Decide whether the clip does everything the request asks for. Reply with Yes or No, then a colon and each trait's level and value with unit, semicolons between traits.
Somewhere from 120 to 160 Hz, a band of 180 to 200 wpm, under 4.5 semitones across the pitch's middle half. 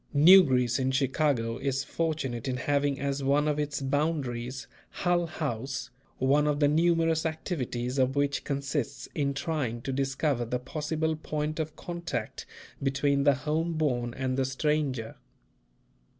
No: medium, 140 Hz; average, 145 wpm; average, 2.8 semitones